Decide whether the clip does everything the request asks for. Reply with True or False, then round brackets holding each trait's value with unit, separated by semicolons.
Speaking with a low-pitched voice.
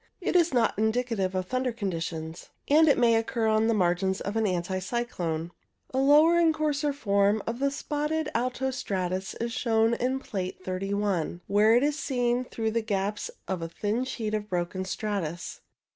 False (220 Hz)